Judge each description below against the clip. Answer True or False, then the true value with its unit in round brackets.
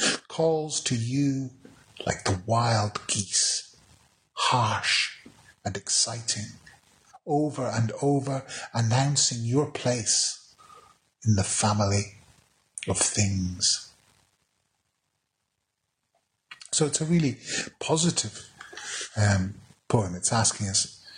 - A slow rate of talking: True (90 wpm)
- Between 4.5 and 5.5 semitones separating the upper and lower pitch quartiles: True (4.9 semitones)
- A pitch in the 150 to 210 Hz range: False (120 Hz)